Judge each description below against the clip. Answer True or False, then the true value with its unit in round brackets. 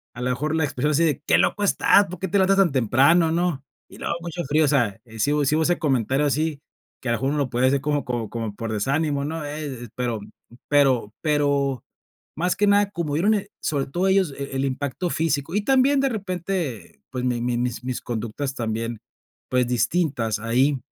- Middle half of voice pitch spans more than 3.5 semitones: True (5.0 semitones)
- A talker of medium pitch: True (145 Hz)